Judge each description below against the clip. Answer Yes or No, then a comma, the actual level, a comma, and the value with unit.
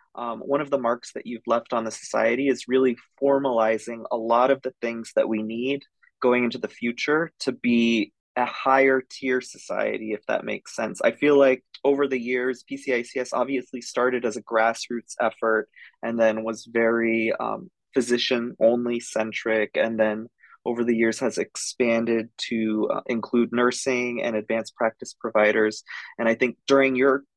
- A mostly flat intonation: Yes, narrow, 2.3 semitones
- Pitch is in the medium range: No, low, 120 Hz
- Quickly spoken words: No, average, 165 wpm